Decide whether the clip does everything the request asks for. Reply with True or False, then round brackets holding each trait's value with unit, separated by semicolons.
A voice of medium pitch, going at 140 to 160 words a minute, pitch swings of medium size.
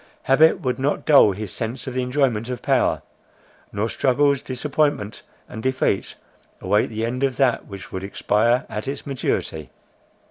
False (125 Hz; 155 wpm; 4.1 semitones)